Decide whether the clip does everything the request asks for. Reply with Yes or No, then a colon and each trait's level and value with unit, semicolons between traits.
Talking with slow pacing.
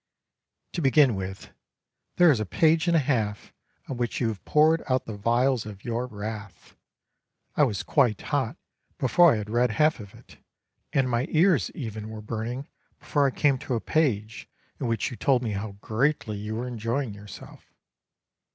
No: average, 180 wpm